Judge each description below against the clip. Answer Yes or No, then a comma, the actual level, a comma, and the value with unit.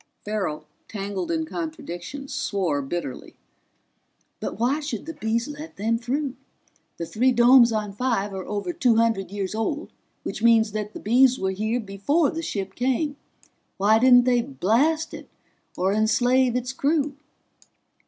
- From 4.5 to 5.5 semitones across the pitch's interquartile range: Yes, average, 4.9 semitones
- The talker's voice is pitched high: Yes, high, 230 Hz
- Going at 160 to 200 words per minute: No, average, 150 wpm